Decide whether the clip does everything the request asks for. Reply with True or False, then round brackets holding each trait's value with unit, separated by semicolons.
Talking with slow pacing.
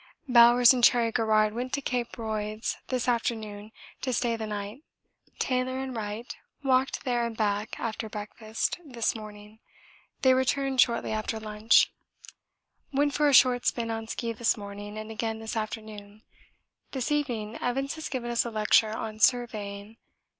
False (155 wpm)